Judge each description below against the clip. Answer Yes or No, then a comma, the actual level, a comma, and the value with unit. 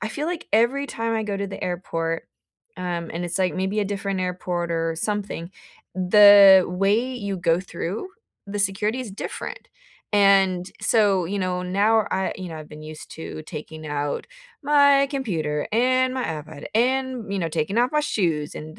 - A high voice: Yes, high, 195 Hz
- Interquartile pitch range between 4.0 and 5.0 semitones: Yes, average, 4.5 semitones